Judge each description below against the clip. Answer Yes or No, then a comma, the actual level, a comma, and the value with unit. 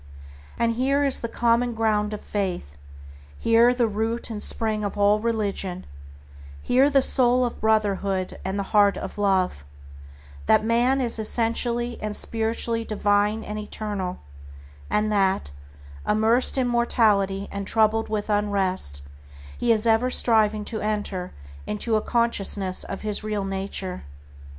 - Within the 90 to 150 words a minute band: Yes, average, 140 wpm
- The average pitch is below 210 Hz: No, high, 215 Hz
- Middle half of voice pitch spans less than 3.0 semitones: Yes, narrow, 2.5 semitones